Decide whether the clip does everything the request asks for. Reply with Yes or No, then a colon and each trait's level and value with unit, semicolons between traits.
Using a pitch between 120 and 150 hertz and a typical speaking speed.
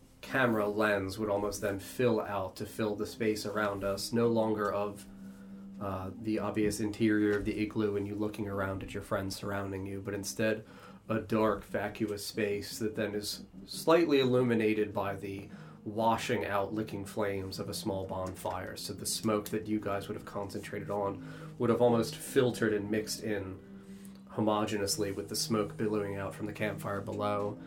No: low, 105 Hz; average, 175 wpm